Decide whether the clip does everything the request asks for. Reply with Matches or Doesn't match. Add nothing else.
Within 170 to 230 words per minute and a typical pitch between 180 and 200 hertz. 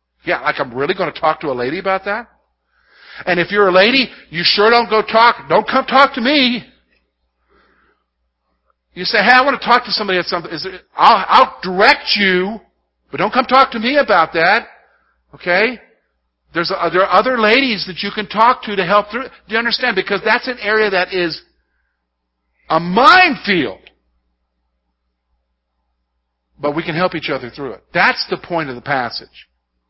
Matches